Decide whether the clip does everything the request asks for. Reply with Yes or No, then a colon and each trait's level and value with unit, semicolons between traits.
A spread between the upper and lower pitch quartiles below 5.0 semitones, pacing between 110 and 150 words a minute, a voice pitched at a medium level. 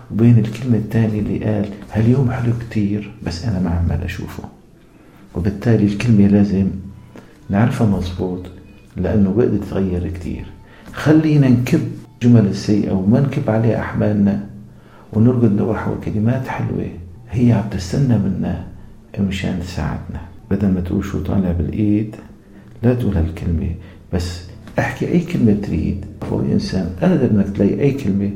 No: narrow, 2.6 semitones; average, 130 wpm; low, 105 Hz